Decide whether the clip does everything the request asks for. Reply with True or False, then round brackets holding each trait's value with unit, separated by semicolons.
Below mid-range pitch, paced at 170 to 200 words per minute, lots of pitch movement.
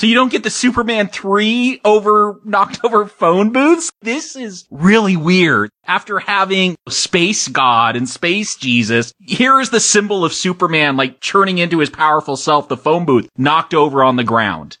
False (185 Hz; 175 wpm; 6.2 semitones)